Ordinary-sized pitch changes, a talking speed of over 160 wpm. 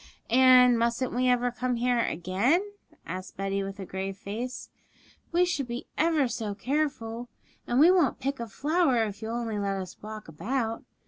Yes: average, 4.2 semitones; average, 175 wpm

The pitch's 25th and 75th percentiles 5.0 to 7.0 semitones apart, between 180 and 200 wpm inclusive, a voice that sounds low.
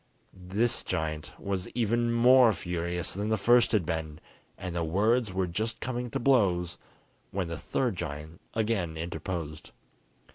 No: wide, 5.4 semitones; average, 140 wpm; very low, 95 Hz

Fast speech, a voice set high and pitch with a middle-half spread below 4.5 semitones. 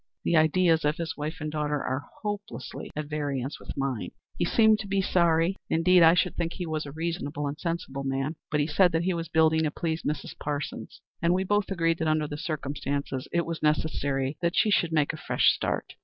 No: fast, 215 wpm; medium, 160 Hz; average, 2.7 semitones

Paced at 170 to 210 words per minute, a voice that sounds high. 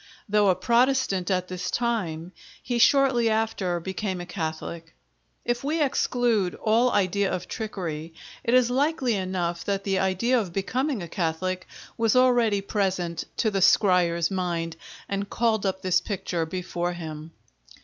No: average, 150 wpm; high, 195 Hz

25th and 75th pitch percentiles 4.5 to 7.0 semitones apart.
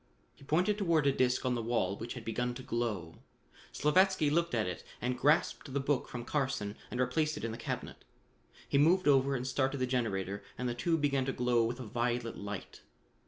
No: average, 3.6 semitones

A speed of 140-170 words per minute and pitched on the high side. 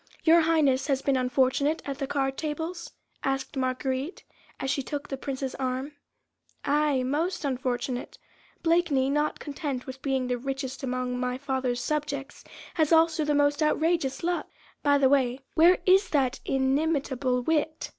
Yes: average, 150 wpm; very high, 275 Hz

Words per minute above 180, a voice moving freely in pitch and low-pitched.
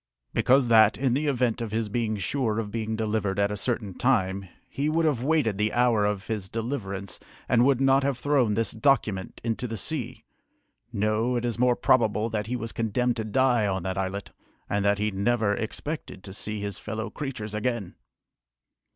No: average, 190 wpm; average, 3.3 semitones; low, 110 Hz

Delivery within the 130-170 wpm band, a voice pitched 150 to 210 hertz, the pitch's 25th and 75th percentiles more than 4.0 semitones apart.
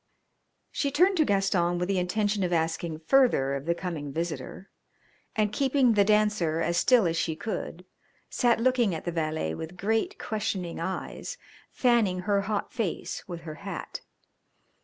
Yes: average, 160 wpm; medium, 185 Hz; average, 4.7 semitones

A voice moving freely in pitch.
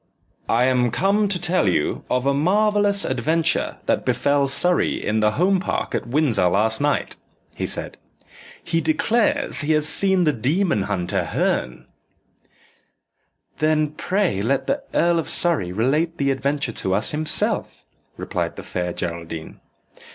Yes: wide, 8.0 semitones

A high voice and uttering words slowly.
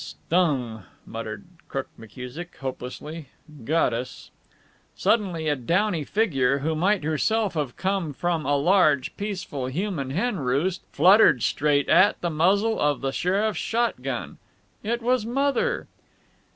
No: medium, 165 Hz; slow, 130 wpm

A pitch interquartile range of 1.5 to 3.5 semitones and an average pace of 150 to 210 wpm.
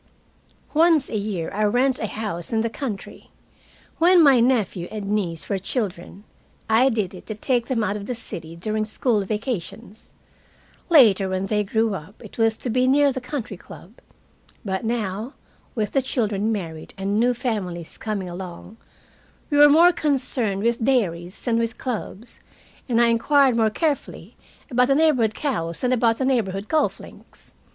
No: average, 4.3 semitones; average, 170 wpm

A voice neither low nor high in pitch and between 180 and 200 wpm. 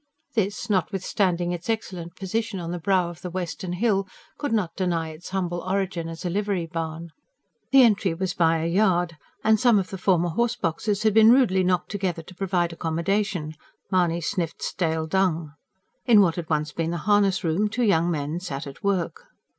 Yes: medium, 180 Hz; average, 185 wpm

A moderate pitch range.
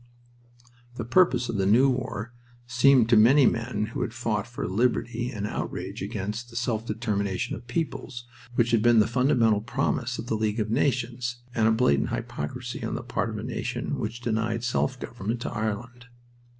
No: narrow, 2.1 semitones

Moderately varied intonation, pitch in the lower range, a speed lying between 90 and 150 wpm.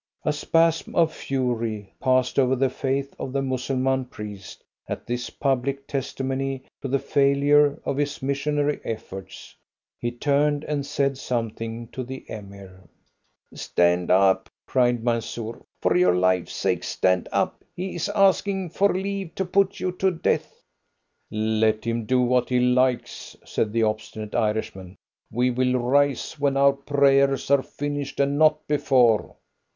Yes: average, 3.8 semitones; low, 130 Hz; average, 145 wpm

